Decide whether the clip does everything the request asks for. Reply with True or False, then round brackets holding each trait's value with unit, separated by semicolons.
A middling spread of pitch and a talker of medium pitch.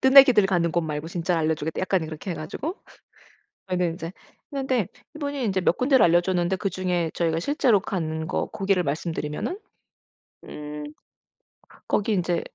True (4.4 semitones; 180 Hz)